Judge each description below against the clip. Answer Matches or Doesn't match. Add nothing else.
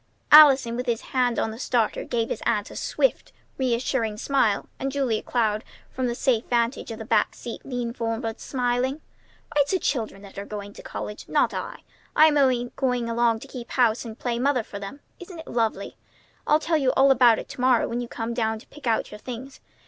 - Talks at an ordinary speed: Doesn't match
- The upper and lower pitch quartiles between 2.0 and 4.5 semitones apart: Matches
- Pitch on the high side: Matches